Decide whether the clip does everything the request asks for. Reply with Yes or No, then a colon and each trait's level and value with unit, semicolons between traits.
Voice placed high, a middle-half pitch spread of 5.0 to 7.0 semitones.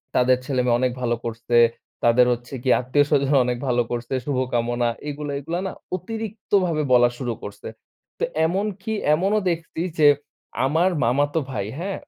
No: low, 135 Hz; wide, 5.6 semitones